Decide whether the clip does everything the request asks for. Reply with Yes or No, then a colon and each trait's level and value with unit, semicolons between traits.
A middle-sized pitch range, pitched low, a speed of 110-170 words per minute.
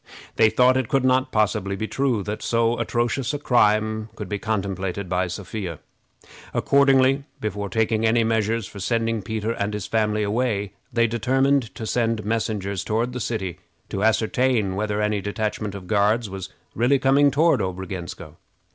Yes: average, 3.0 semitones; low, 110 Hz; average, 160 wpm